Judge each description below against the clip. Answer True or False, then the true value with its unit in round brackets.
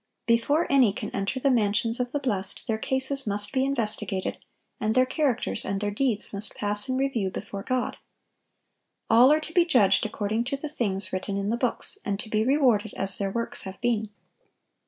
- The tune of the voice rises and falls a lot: False (4.3 semitones)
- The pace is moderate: True (195 wpm)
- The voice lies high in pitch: True (225 Hz)